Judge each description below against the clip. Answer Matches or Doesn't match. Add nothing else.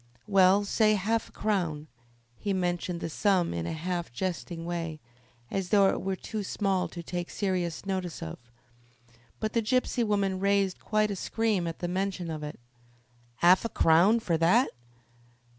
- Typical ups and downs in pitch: Matches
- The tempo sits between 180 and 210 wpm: Doesn't match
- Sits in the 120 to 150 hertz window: Doesn't match